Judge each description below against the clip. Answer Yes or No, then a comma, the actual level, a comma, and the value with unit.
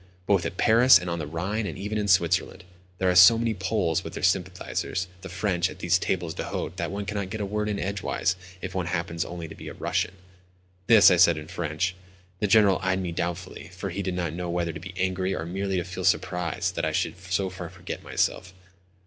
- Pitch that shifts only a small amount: Yes, narrow, 2.2 semitones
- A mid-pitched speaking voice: No, very low, 90 Hz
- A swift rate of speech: Yes, fast, 225 wpm